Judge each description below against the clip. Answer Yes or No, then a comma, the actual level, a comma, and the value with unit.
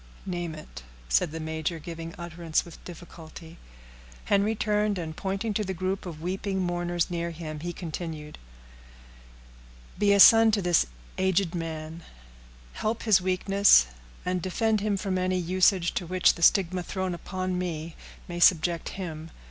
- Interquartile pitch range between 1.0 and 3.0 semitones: Yes, narrow, 2.5 semitones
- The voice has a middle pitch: Yes, medium, 175 Hz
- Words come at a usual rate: Yes, average, 150 wpm